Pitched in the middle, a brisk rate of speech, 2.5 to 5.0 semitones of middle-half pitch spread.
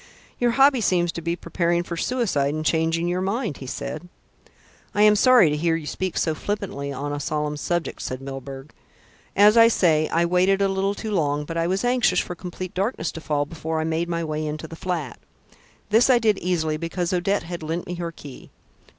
Yes: medium, 170 Hz; fast, 210 wpm; average, 3.9 semitones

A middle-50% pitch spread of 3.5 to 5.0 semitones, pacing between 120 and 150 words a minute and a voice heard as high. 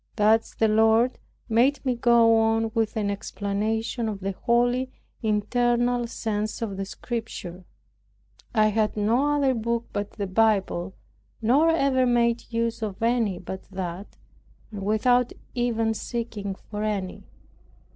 No: narrow, 2.6 semitones; slow, 135 wpm; high, 225 Hz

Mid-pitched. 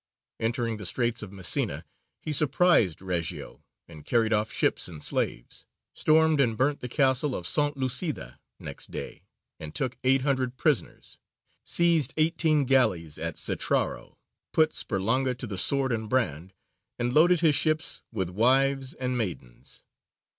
No: low, 125 Hz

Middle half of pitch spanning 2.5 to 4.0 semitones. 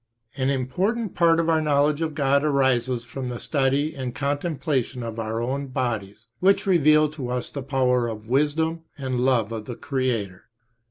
Yes: average, 3.7 semitones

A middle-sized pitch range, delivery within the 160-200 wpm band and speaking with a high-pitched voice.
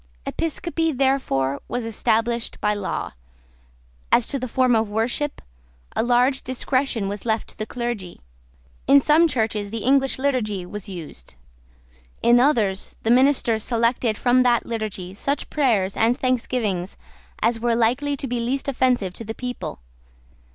No: average, 3.3 semitones; average, 145 wpm; high, 235 Hz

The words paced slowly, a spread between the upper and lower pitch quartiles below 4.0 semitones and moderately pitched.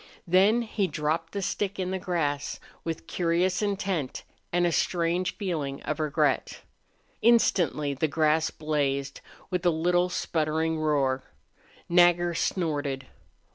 Yes: slow, 125 wpm; average, 3.1 semitones; medium, 165 Hz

